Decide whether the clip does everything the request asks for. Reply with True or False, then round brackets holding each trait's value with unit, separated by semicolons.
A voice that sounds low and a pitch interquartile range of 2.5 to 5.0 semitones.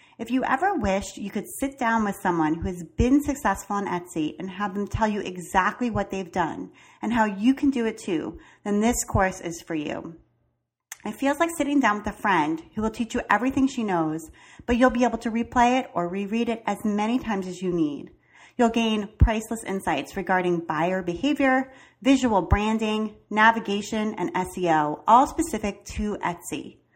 False (210 Hz; 4.5 semitones)